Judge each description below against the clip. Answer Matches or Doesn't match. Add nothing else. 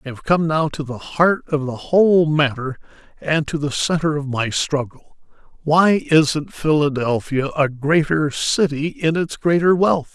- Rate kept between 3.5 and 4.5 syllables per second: Matches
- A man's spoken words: Matches